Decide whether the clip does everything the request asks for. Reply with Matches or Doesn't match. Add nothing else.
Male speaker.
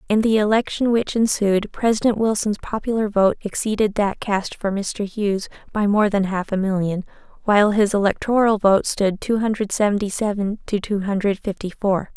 Doesn't match